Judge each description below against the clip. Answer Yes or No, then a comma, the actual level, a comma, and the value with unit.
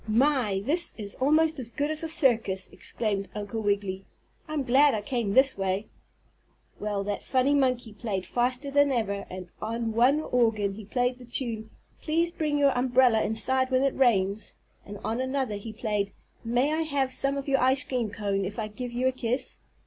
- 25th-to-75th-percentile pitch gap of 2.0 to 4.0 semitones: No, average, 4.5 semitones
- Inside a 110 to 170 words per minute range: No, average, 185 wpm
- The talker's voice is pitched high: Yes, high, 245 Hz